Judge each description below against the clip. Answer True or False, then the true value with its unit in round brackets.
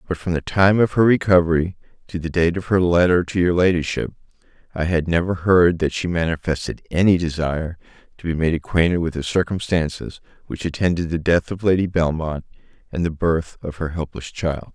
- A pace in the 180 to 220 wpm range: True (185 wpm)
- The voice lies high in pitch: False (85 Hz)